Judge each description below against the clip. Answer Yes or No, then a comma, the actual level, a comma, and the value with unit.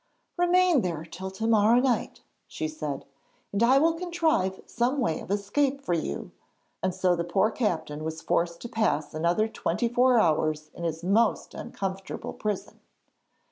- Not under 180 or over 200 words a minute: No, average, 160 wpm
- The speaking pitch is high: Yes, high, 200 Hz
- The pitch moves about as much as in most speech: No, wide, 6.3 semitones